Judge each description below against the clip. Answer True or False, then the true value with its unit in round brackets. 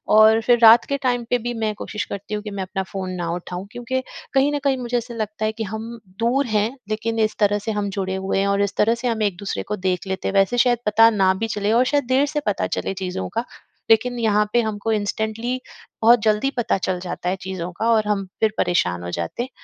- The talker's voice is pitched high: True (215 Hz)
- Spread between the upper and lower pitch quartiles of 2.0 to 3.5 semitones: True (3.1 semitones)